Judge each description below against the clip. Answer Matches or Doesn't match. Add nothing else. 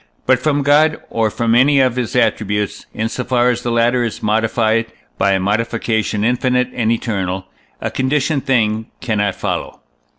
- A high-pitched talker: Doesn't match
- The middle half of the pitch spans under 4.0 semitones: Matches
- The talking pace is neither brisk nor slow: Matches